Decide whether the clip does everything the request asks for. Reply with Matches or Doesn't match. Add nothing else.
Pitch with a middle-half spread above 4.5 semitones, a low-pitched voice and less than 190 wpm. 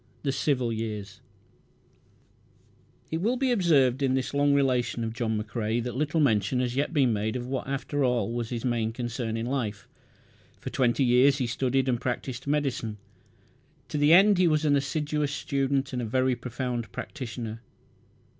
Doesn't match